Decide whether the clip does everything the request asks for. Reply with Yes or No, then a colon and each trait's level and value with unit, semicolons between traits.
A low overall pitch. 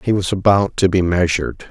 Yes: very low, 90 Hz